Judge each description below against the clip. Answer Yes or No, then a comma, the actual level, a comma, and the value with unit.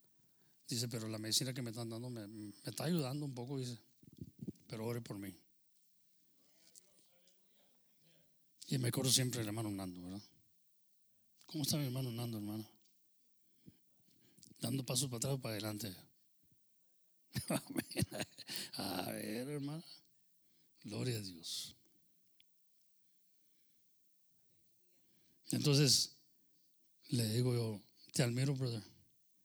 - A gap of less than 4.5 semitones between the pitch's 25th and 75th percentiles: No, average, 4.8 semitones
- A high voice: No, low, 125 Hz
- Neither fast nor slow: No, slow, 110 wpm